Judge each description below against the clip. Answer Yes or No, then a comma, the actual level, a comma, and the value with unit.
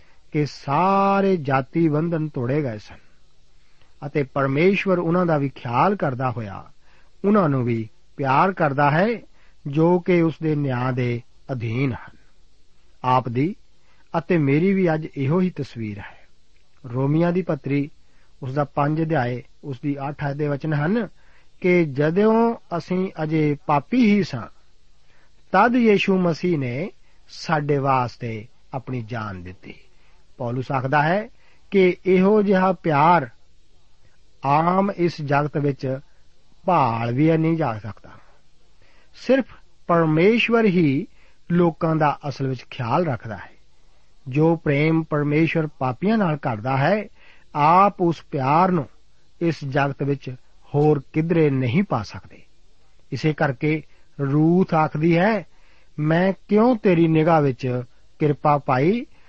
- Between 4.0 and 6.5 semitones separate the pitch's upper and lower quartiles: Yes, average, 5.3 semitones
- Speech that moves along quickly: No, average, 125 wpm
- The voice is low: No, medium, 150 Hz